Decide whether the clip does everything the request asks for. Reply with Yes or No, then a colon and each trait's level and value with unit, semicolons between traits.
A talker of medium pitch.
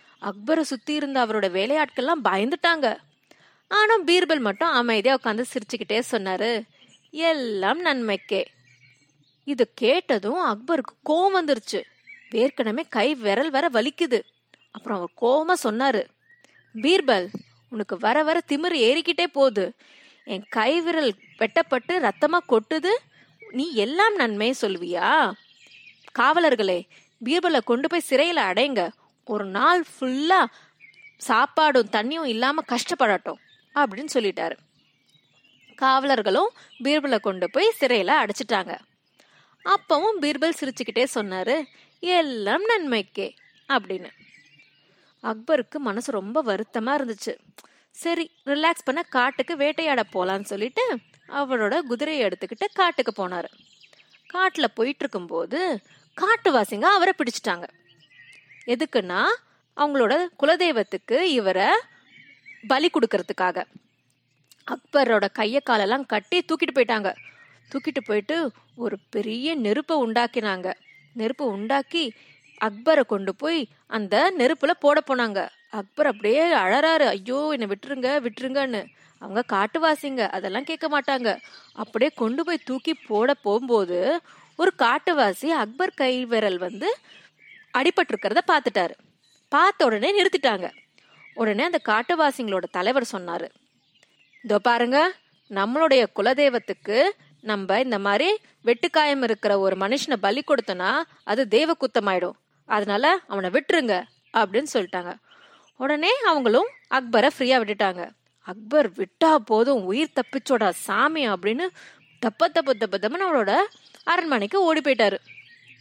No: very high, 260 Hz